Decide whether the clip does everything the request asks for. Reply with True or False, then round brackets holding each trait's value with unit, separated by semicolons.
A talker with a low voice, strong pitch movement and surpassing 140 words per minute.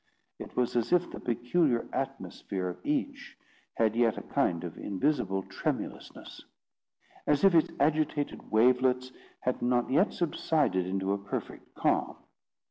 False (125 Hz; 7.2 semitones; 135 wpm)